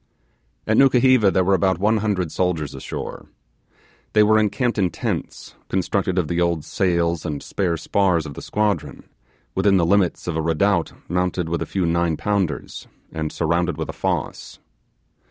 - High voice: No, very low, 90 Hz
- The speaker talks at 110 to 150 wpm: No, average, 165 wpm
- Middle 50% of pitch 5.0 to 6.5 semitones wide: No, average, 3.2 semitones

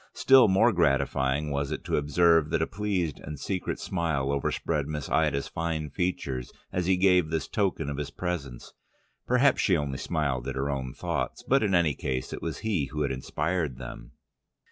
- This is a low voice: Yes, very low, 75 Hz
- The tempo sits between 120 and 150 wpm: No, average, 185 wpm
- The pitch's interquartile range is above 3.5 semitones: Yes, average, 4.6 semitones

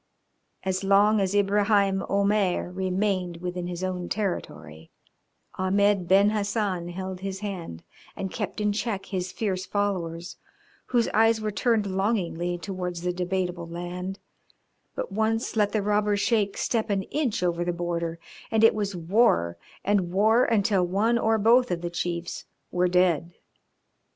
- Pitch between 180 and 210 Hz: Yes, high, 190 Hz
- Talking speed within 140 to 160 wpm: Yes, average, 145 wpm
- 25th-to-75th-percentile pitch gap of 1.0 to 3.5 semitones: Yes, average, 2.9 semitones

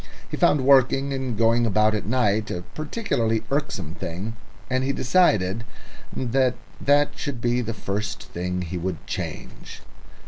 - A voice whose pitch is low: Yes, low, 115 Hz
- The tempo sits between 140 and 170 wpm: Yes, average, 145 wpm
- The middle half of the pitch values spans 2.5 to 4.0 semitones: No, average, 4.7 semitones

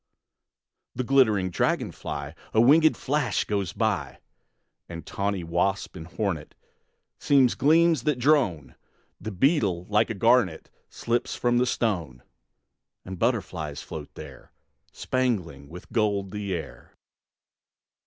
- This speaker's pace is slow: Yes, slow, 120 wpm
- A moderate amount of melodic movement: No, wide, 6.2 semitones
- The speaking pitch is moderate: No, low, 105 Hz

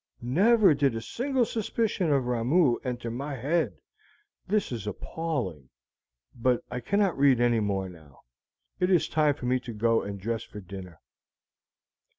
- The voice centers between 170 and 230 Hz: No, low, 125 Hz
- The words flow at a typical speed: Yes, average, 155 wpm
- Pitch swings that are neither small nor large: No, wide, 6.7 semitones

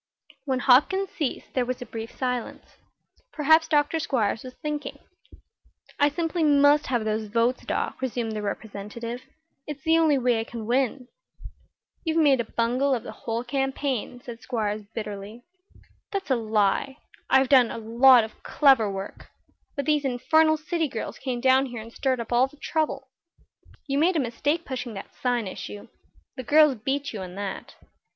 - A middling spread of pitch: Yes, average, 4.1 semitones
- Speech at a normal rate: Yes, average, 170 wpm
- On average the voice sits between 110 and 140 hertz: No, very high, 255 Hz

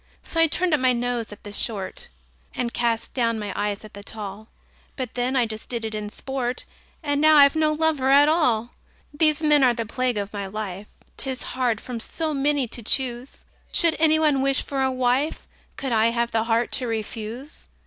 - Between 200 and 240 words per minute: Yes, fast, 205 wpm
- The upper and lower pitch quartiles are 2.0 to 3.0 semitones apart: No, average, 4.3 semitones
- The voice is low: No, very high, 250 Hz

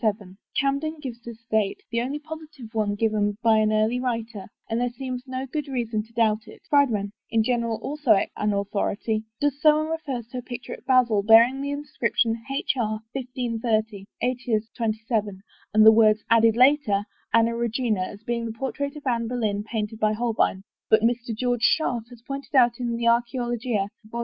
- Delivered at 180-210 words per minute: Yes, average, 185 wpm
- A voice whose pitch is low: No, high, 235 Hz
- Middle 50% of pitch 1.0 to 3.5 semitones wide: Yes, average, 2.7 semitones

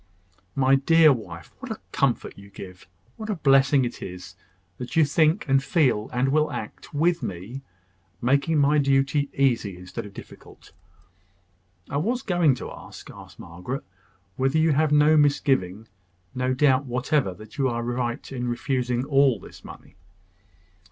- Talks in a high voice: No, low, 135 Hz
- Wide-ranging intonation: No, average, 3.7 semitones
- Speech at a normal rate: Yes, average, 150 wpm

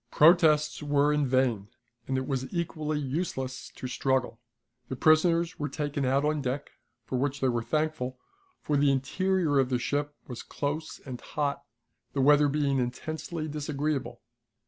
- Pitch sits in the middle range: Yes, medium, 145 Hz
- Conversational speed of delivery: Yes, average, 155 wpm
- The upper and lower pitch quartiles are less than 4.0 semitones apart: Yes, narrow, 2.6 semitones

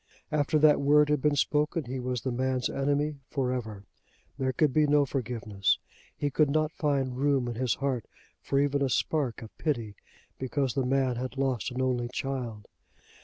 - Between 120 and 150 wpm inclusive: No, average, 180 wpm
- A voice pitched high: No, low, 135 Hz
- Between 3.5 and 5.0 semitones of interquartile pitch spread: No, narrow, 2.5 semitones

